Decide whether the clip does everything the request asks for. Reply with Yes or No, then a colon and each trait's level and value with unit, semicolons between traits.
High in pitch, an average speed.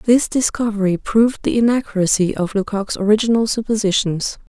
No: high, 215 Hz; slow, 120 wpm